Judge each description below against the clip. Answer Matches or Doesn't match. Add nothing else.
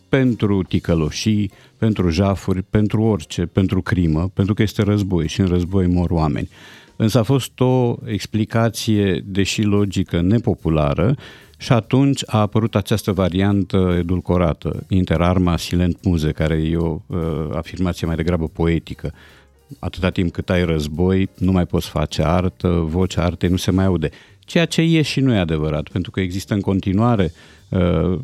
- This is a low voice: Matches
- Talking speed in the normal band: Matches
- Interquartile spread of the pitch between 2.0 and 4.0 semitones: Matches